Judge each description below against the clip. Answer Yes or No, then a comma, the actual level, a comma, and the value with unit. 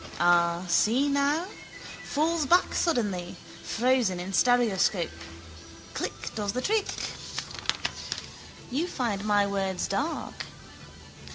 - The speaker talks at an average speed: No, slow, 95 wpm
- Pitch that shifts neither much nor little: No, wide, 6.8 semitones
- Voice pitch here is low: No, high, 225 Hz